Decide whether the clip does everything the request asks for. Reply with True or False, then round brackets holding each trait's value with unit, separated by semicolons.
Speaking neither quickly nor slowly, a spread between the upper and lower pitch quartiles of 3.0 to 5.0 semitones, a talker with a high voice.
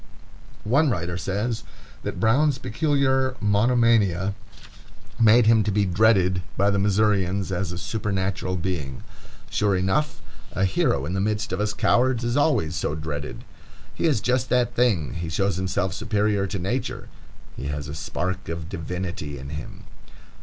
False (155 wpm; 4.5 semitones; 100 Hz)